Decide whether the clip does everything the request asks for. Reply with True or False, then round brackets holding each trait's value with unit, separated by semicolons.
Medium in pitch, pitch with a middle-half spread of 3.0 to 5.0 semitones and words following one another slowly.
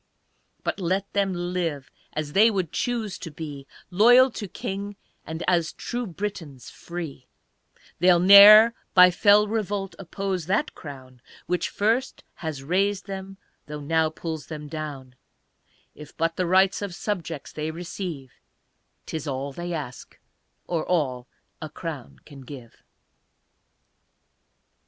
True (175 Hz; 4.7 semitones; 130 wpm)